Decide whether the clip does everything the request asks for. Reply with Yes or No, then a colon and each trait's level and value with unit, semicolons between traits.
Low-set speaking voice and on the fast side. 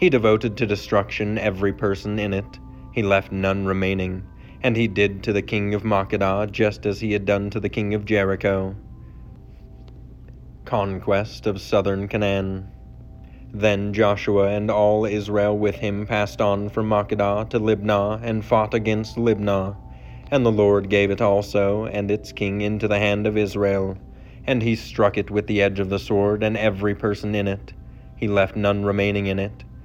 No: low, 105 Hz; average, 175 wpm